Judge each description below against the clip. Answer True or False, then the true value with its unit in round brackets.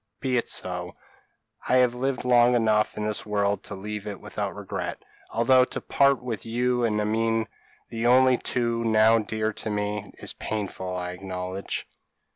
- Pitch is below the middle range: True (110 Hz)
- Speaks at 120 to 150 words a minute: False (165 wpm)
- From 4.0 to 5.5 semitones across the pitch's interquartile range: False (2.9 semitones)